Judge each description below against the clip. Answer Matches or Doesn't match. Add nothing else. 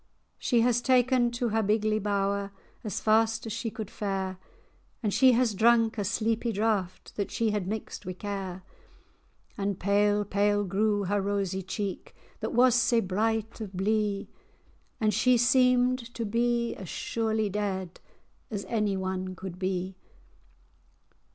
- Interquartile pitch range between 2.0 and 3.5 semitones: Matches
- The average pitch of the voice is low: Doesn't match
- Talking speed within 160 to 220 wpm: Doesn't match